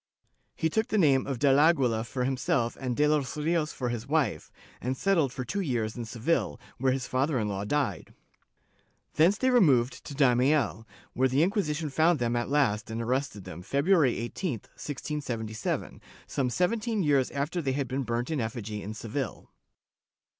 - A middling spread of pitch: Yes, average, 4.4 semitones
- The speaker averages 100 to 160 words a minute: No, average, 175 wpm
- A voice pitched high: No, low, 135 Hz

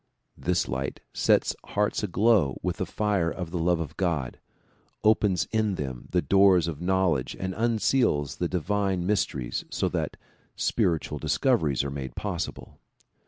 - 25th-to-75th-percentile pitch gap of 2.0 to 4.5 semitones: No, average, 5.2 semitones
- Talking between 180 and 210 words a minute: No, average, 145 wpm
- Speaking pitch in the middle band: No, very low, 90 Hz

